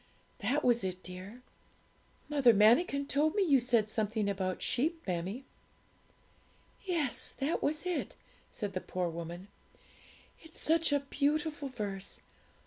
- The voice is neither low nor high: No, high, 245 Hz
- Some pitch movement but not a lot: No, wide, 7.1 semitones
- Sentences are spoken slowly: Yes, slow, 130 wpm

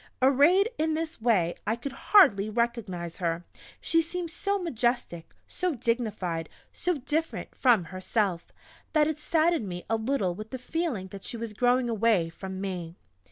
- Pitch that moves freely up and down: Yes, wide, 8.5 semitones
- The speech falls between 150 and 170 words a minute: Yes, average, 160 wpm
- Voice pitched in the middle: No, high, 235 Hz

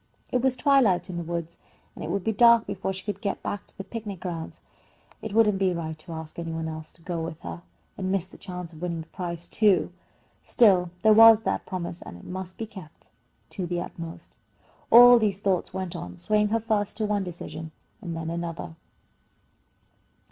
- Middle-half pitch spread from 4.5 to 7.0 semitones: No, average, 3.8 semitones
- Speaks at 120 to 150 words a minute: No, fast, 205 wpm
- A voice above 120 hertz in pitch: Yes, medium, 185 Hz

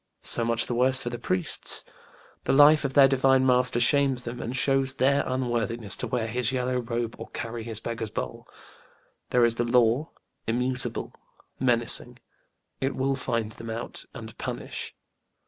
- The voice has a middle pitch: No, low, 125 Hz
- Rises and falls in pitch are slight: Yes, narrow, 2.2 semitones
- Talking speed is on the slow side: No, average, 165 wpm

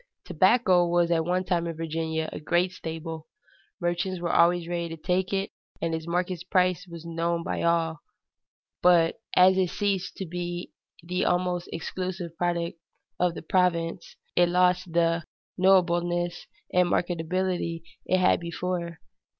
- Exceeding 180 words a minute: No, average, 145 wpm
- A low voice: No, medium, 175 Hz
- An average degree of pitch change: No, narrow, 1.4 semitones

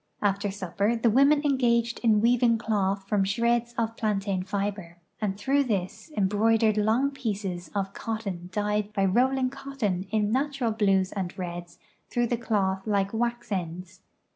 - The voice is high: Yes, high, 210 Hz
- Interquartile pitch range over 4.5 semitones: No, average, 3.4 semitones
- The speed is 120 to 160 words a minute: Yes, average, 150 wpm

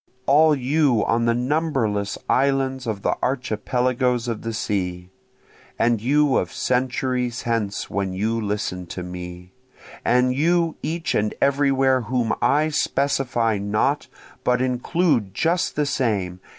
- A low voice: Yes, low, 125 Hz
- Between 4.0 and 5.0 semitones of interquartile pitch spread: Yes, average, 4.5 semitones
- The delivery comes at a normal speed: No, slow, 130 wpm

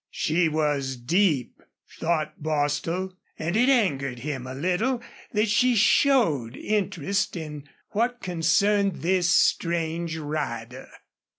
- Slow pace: Yes, slow, 110 wpm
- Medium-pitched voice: Yes, medium, 165 Hz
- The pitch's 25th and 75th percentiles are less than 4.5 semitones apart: No, average, 5.3 semitones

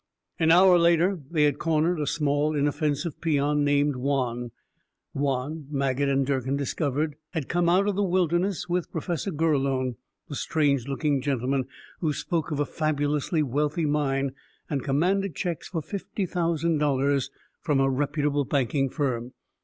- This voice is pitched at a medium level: Yes, medium, 145 Hz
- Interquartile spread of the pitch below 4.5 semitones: Yes, average, 3.1 semitones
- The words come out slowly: No, average, 155 wpm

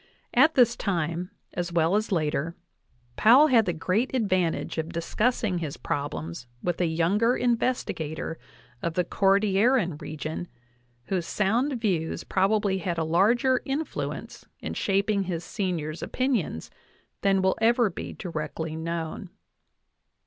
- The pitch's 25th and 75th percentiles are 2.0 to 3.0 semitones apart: No, average, 5.1 semitones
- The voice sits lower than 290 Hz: Yes, medium, 185 Hz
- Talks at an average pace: No, slow, 130 wpm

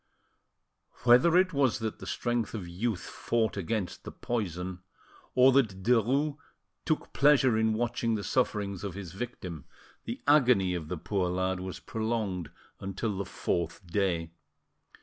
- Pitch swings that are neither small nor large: Yes, average, 4.6 semitones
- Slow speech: No, average, 145 wpm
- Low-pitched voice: Yes, low, 105 Hz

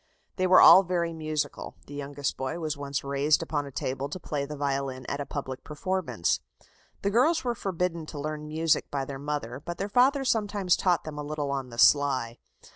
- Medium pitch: Yes, medium, 150 Hz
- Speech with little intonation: No, average, 4.1 semitones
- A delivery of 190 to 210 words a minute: Yes, average, 200 wpm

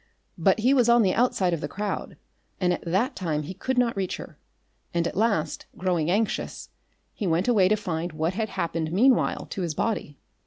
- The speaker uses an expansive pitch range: No, average, 4.9 semitones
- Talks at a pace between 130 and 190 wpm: No, average, 200 wpm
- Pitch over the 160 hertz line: Yes, medium, 185 Hz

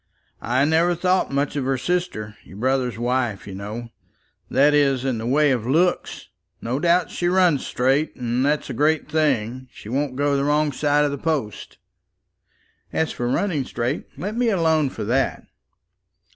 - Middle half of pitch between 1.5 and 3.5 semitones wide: No, average, 4.0 semitones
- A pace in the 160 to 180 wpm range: Yes, average, 170 wpm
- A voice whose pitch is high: No, medium, 140 Hz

